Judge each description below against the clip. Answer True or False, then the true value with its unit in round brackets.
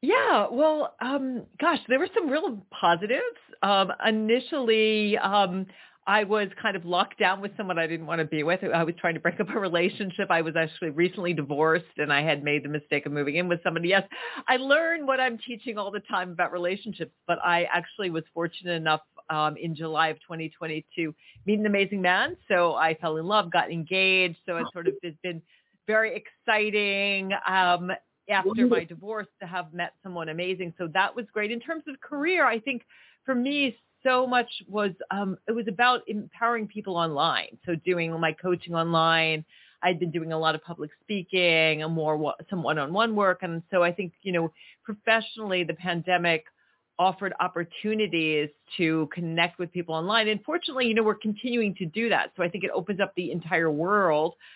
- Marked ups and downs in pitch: False (4.5 semitones)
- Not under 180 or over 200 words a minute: True (190 wpm)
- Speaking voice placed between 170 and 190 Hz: True (185 Hz)